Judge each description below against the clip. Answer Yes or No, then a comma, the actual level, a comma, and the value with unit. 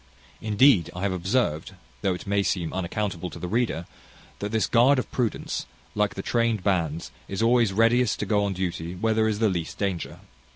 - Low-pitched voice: Yes, low, 100 Hz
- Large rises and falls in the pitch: No, average, 3.9 semitones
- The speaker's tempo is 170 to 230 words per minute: Yes, average, 195 wpm